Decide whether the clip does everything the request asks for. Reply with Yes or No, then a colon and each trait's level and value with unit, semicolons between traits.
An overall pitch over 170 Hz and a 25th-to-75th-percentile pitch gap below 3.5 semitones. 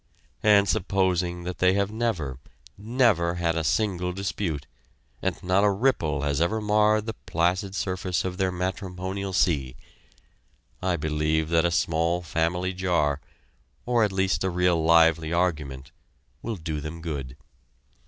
No: very low, 90 Hz; average, 3.0 semitones